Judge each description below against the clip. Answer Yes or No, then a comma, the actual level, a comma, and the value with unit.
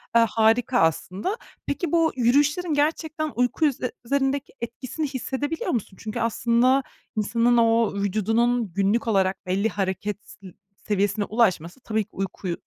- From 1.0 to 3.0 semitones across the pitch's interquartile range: No, average, 4.8 semitones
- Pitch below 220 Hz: No, high, 230 Hz